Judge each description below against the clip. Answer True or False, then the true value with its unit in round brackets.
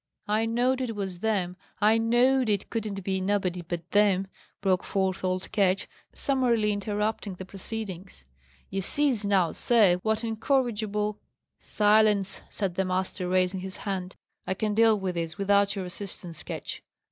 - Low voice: False (200 Hz)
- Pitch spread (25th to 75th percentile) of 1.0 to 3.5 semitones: True (2.8 semitones)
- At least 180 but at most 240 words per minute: False (155 wpm)